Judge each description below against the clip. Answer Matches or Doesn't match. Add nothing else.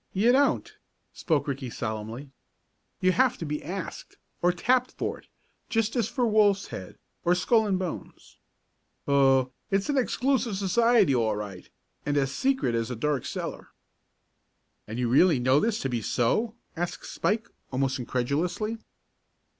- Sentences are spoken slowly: Doesn't match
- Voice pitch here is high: Doesn't match